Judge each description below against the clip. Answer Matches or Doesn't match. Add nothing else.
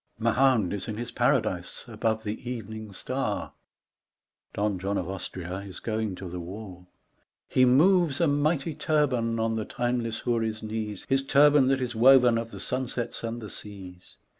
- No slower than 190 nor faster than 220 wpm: Doesn't match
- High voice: Doesn't match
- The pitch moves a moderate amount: Matches